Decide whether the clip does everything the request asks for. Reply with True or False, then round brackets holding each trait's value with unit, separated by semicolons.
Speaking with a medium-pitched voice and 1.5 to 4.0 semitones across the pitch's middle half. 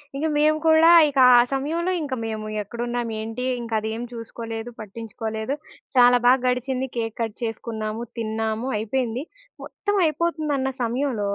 False (240 Hz; 3.4 semitones)